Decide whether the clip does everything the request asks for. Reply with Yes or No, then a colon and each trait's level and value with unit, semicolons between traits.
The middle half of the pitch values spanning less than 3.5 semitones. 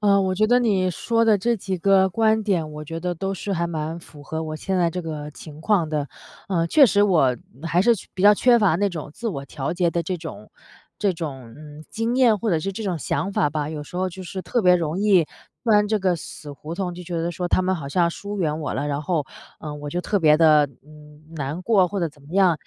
No: average, 4.3 semitones